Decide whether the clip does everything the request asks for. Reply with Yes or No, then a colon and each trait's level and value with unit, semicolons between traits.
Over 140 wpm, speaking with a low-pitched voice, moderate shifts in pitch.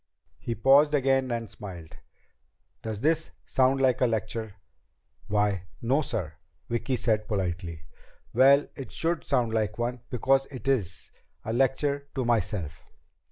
No: slow, 135 wpm; low, 120 Hz; average, 4.4 semitones